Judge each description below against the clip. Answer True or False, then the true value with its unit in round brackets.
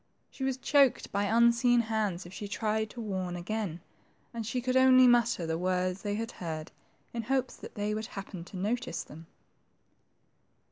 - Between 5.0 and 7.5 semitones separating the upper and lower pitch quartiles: False (4.4 semitones)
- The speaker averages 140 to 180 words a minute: True (160 wpm)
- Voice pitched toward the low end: False (215 Hz)